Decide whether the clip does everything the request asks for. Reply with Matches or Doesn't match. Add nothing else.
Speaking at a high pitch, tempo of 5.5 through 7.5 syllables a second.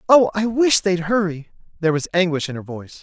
Doesn't match